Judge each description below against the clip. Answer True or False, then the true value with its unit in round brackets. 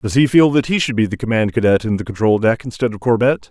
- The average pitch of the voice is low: True (115 Hz)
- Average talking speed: False (290 wpm)